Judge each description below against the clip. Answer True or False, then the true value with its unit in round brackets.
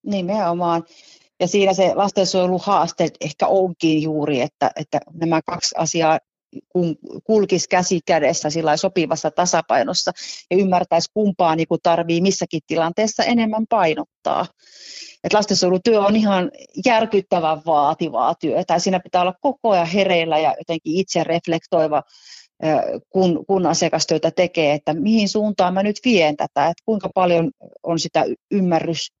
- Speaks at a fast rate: False (130 wpm)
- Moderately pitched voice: True (175 Hz)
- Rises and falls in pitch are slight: False (3.2 semitones)